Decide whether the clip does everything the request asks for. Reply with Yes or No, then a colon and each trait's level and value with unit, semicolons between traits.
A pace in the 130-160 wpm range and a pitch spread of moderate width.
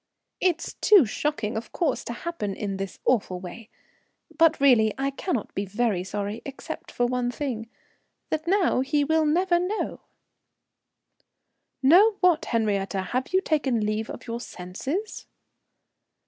No: average, 140 wpm; wide, 7.1 semitones